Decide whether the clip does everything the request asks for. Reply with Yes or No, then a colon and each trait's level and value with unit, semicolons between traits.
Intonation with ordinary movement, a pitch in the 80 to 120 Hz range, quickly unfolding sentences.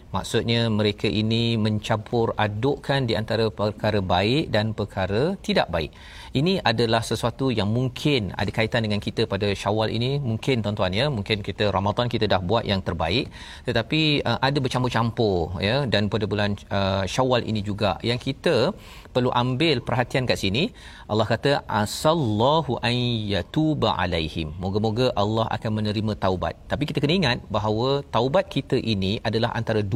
Yes: average, 3.5 semitones; low, 110 Hz; fast, 150 wpm